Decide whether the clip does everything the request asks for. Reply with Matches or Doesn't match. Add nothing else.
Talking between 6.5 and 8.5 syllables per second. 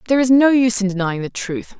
Matches